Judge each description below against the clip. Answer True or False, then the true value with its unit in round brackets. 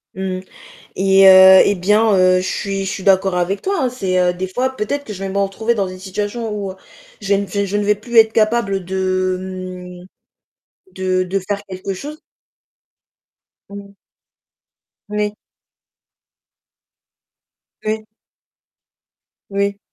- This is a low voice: False (195 Hz)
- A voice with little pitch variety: True (2.0 semitones)